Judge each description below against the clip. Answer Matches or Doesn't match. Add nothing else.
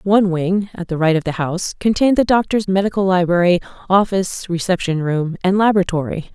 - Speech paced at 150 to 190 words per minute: Matches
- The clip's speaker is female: Matches